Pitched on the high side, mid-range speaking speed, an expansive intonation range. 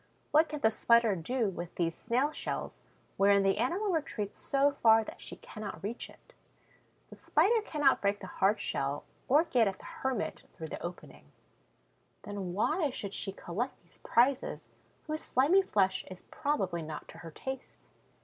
Yes: high, 220 Hz; average, 170 wpm; wide, 6.6 semitones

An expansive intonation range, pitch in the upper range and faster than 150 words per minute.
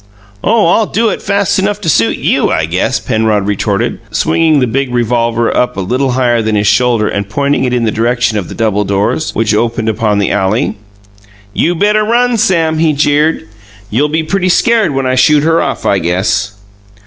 No: wide, 6.9 semitones; low, 125 Hz; average, 195 wpm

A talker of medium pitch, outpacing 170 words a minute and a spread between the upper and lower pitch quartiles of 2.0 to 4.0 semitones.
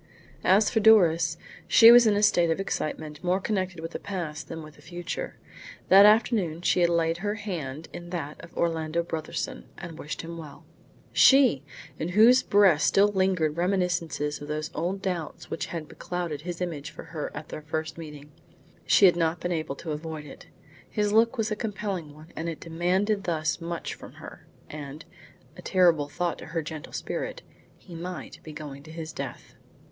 Yes: medium, 170 Hz; average, 190 wpm; average, 3.5 semitones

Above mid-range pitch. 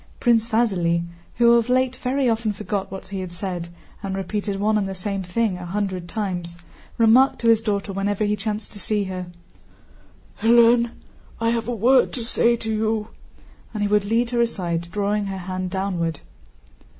Yes: high, 210 Hz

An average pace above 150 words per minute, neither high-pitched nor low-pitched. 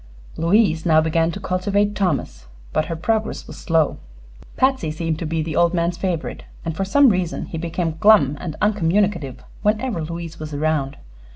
Yes: average, 170 wpm; medium, 170 Hz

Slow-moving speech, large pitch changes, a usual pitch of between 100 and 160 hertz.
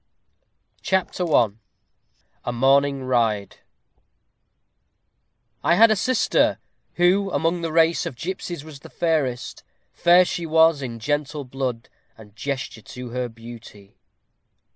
Yes: slow, 120 wpm; wide, 5.8 semitones; medium, 140 Hz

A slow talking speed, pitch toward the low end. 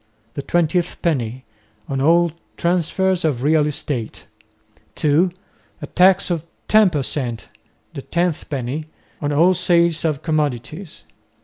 No: slow, 125 wpm; medium, 155 Hz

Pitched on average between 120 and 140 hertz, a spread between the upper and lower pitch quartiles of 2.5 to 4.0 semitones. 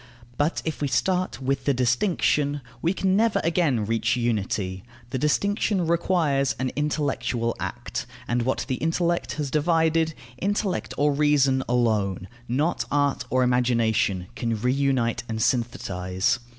No: low, 135 Hz; wide, 5.4 semitones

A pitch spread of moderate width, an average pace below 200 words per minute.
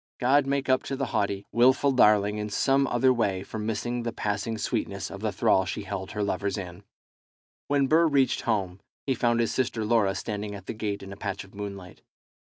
No: average, 4.4 semitones; fast, 205 wpm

